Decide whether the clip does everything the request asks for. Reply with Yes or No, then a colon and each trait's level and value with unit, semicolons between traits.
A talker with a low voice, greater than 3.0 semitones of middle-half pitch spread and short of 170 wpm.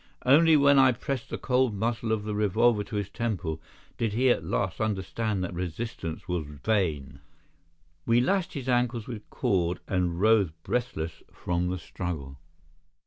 Yes: low, 105 Hz; average, 5.3 semitones; average, 155 wpm